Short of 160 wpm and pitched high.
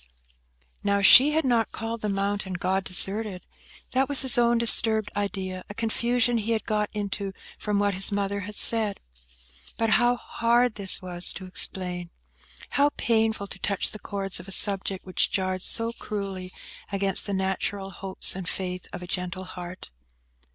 No: average, 165 wpm; high, 200 Hz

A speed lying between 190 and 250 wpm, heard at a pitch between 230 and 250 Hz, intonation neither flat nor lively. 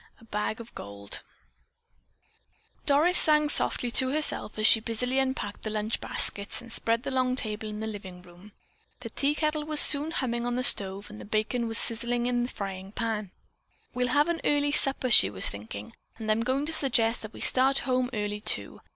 Yes: average, 195 wpm; high, 235 Hz; average, 3.8 semitones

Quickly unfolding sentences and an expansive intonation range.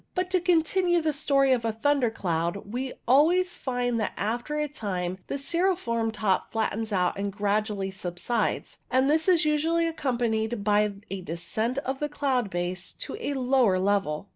No: average, 165 wpm; wide, 6.5 semitones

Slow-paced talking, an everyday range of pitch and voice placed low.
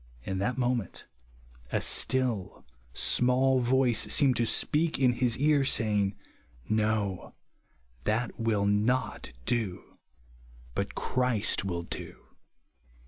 Yes: slow, 115 wpm; average, 3.8 semitones; low, 120 Hz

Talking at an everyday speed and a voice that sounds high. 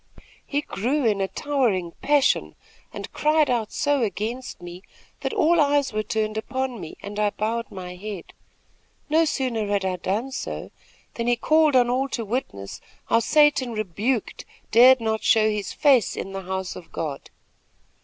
Yes: average, 165 wpm; high, 230 Hz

